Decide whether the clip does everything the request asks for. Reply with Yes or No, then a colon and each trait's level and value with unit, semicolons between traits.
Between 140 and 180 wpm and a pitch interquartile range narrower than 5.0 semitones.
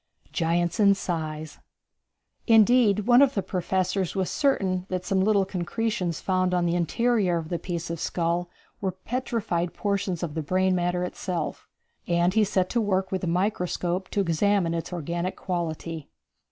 Yes: average, 160 wpm; narrow, 2.6 semitones